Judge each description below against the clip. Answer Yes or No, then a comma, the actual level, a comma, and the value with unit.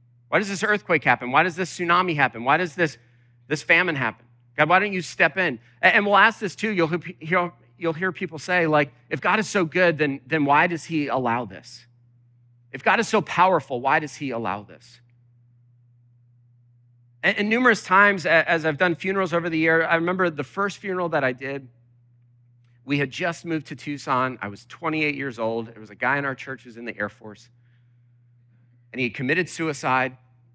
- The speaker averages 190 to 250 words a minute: Yes, fast, 205 wpm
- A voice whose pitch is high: No, medium, 140 Hz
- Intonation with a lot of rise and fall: Yes, wide, 6.1 semitones